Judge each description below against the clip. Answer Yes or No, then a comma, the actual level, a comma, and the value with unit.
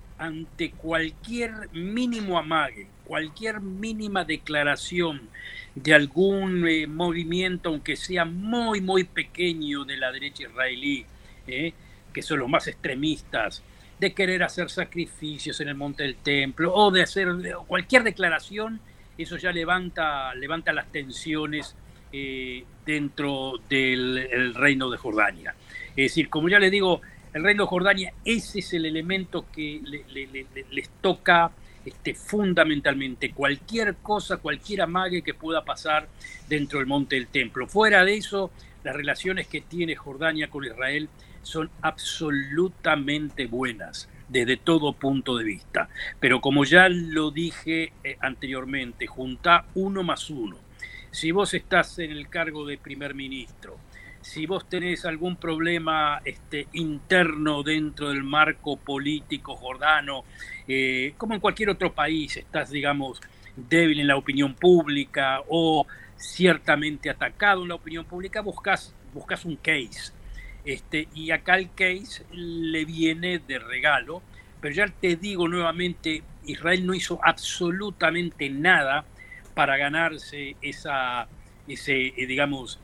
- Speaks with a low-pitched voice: No, medium, 155 Hz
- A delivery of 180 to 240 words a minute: No, average, 135 wpm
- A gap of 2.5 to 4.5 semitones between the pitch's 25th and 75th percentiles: Yes, average, 4.2 semitones